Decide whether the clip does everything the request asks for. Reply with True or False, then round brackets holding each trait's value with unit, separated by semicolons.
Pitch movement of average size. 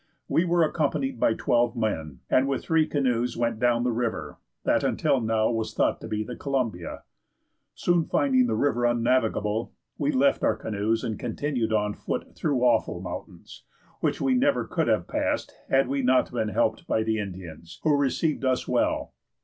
True (3.9 semitones)